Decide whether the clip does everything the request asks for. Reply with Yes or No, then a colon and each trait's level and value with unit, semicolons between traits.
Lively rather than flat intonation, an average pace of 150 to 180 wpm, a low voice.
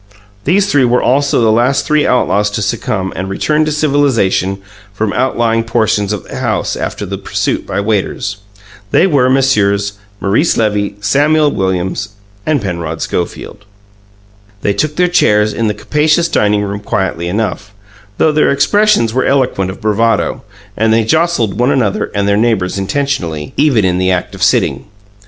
Yes: wide, 5.7 semitones; average, 160 wpm; low, 110 Hz